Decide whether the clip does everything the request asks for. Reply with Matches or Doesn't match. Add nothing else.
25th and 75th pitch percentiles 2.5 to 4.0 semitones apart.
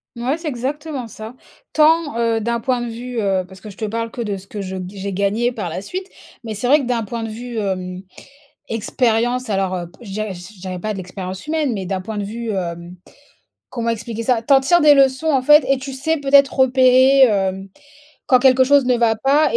Doesn't match